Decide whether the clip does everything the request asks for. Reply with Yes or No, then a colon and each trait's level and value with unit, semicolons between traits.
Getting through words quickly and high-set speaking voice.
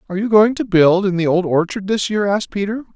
Yes: fast, 265 wpm; high, 195 Hz